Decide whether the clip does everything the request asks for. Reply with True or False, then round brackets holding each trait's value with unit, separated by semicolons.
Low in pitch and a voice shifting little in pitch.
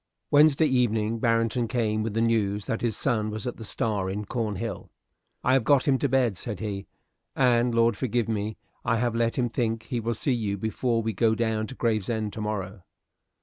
True (115 Hz; 2.1 semitones)